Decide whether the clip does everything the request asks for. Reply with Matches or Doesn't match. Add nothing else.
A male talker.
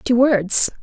Doesn't match